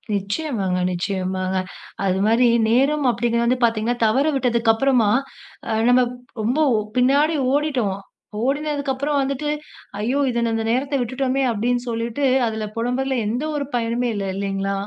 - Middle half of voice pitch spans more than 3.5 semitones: Yes, average, 3.9 semitones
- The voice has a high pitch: Yes, high, 240 Hz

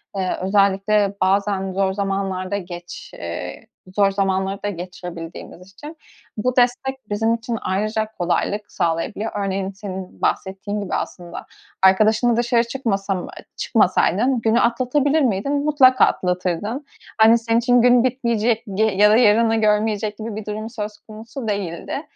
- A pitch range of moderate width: Yes, average, 3.3 semitones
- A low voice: No, high, 210 Hz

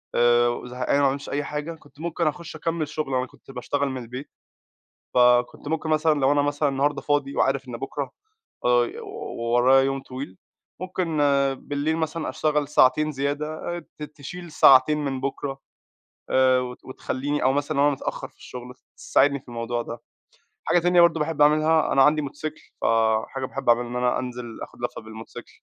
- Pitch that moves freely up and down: No, average, 3.1 semitones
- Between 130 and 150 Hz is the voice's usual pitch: Yes, medium, 140 Hz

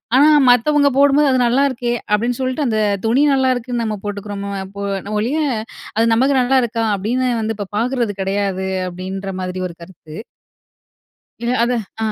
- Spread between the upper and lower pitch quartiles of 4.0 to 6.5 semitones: Yes, average, 4.3 semitones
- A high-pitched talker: Yes, high, 235 Hz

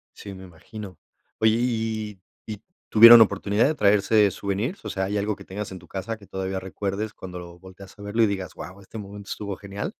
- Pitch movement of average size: No, narrow, 2.1 semitones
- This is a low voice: Yes, low, 100 Hz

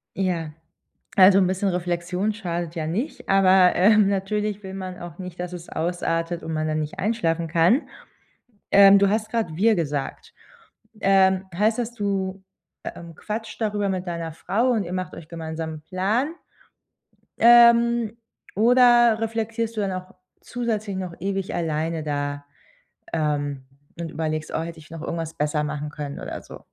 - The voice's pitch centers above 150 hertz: Yes, medium, 185 Hz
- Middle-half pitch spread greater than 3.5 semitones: Yes, average, 4.3 semitones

